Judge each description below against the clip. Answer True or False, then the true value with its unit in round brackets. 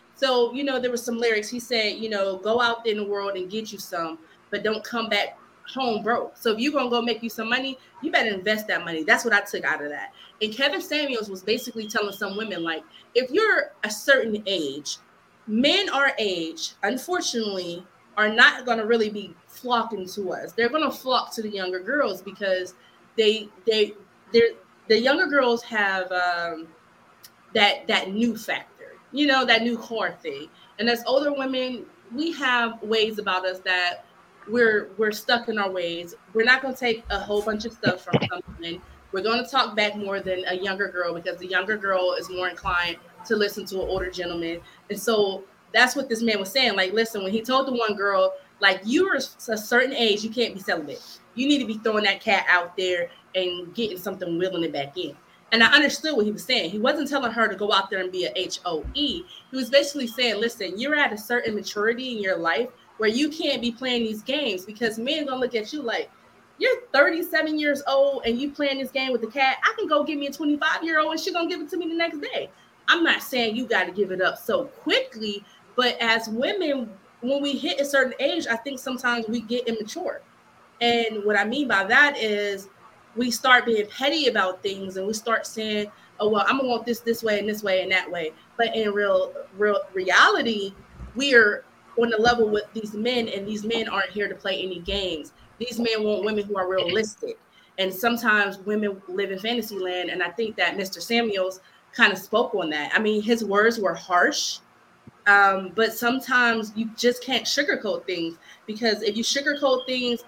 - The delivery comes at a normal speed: False (215 wpm)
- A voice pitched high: True (225 Hz)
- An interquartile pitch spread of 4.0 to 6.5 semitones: True (4.5 semitones)